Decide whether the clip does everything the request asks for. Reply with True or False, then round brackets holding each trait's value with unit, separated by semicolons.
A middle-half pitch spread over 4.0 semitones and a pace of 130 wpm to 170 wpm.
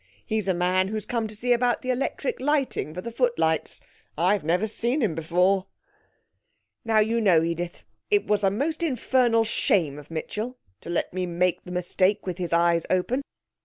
False (5.3 semitones; 185 wpm)